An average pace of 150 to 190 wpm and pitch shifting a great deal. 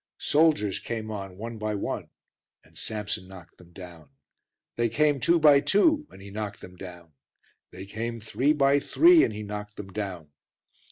Yes: average, 170 wpm; wide, 6.3 semitones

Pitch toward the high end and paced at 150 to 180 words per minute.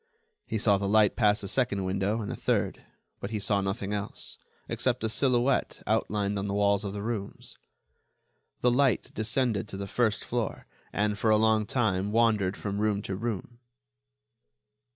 No: low, 105 Hz; average, 175 wpm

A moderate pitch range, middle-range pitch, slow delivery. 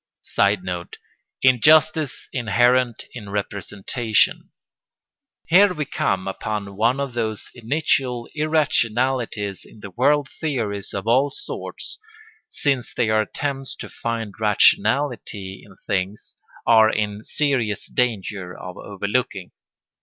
No: average, 4.6 semitones; low, 115 Hz; slow, 110 wpm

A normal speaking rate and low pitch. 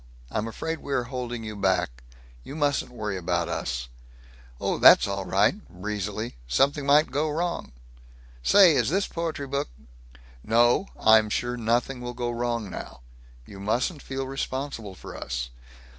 Yes: average, 155 wpm; low, 120 Hz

